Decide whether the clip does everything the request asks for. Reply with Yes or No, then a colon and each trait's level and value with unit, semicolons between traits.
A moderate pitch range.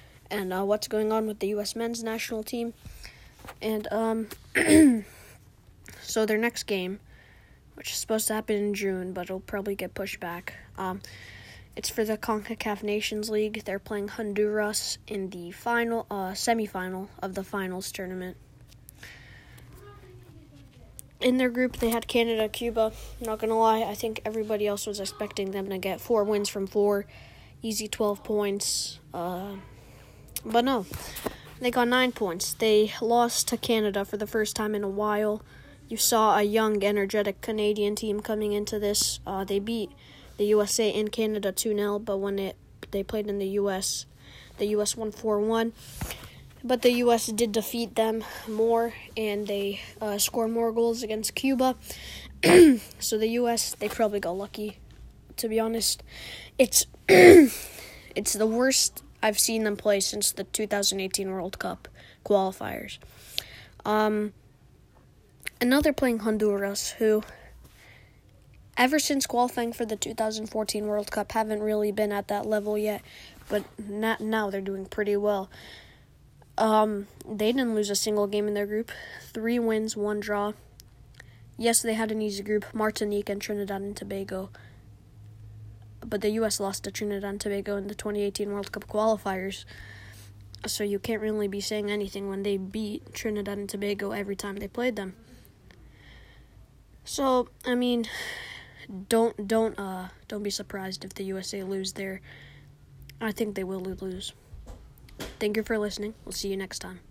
No: narrow, 2.2 semitones